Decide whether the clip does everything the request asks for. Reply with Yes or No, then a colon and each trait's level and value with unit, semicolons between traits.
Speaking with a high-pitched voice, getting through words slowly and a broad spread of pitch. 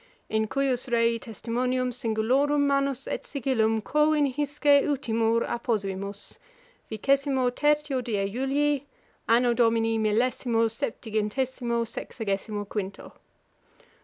No: high, 240 Hz; slow, 100 wpm; average, 3.7 semitones